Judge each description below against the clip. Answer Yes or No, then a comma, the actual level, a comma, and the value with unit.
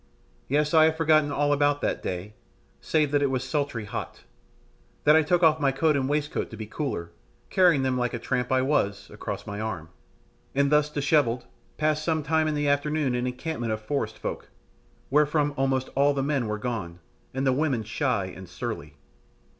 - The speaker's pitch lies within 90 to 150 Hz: Yes, medium, 140 Hz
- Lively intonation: No, average, 4.4 semitones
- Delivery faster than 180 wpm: Yes, average, 190 wpm